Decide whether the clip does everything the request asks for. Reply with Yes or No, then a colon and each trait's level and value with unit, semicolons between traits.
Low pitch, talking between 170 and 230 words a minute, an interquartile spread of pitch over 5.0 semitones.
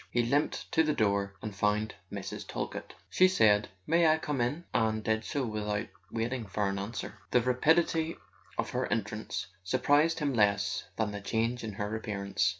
Yes: low, 110 Hz; average, 175 wpm; wide, 5.6 semitones